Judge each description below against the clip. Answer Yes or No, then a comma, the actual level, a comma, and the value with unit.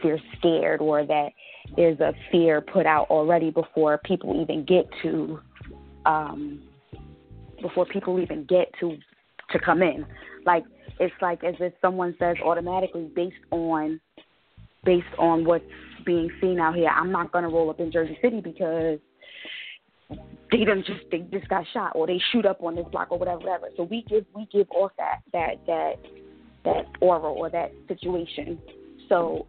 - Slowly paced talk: No, average, 165 wpm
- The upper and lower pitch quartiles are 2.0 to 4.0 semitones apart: Yes, narrow, 2.5 semitones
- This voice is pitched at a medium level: Yes, medium, 170 Hz